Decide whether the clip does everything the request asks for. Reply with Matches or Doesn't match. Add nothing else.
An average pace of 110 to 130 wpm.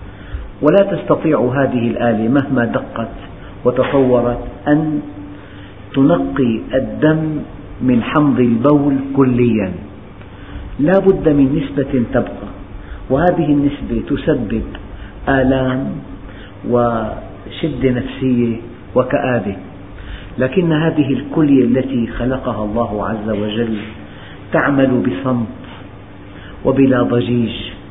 Doesn't match